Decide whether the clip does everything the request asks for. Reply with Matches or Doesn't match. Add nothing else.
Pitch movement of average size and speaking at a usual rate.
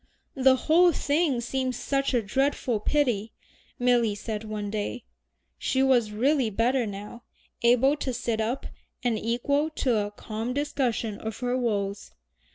Matches